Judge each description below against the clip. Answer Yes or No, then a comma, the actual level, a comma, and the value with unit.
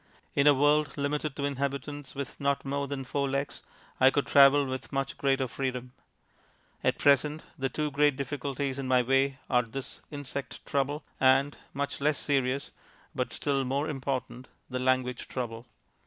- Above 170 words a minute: No, average, 160 wpm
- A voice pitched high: No, medium, 140 Hz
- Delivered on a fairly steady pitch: Yes, narrow, 1.5 semitones